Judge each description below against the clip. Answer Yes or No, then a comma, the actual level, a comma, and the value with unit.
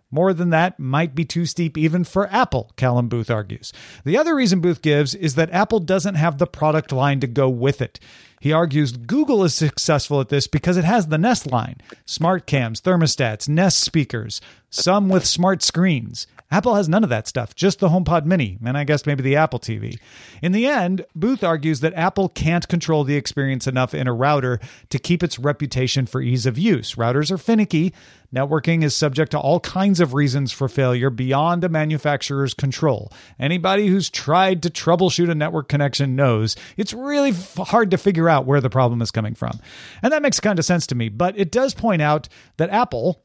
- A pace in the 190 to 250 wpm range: Yes, fast, 205 wpm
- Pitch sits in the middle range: Yes, medium, 155 Hz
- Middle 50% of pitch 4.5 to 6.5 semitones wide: Yes, wide, 5.4 semitones